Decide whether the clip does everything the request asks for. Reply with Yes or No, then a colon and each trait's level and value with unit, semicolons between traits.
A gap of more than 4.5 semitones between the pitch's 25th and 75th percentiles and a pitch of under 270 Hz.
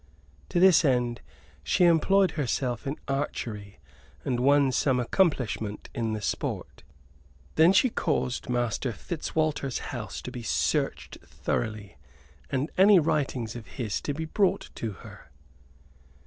Yes: average, 5.2 semitones; low, 135 Hz